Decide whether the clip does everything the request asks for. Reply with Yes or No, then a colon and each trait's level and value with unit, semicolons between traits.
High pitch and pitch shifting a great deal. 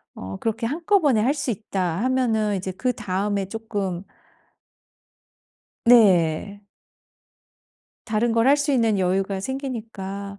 No: high, 215 Hz; average, 4.1 semitones